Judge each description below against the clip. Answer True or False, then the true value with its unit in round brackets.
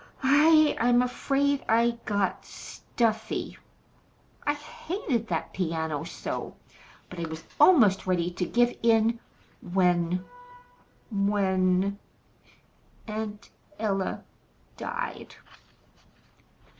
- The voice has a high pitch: True (215 Hz)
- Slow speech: True (85 wpm)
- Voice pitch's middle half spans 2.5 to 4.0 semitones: False (5.0 semitones)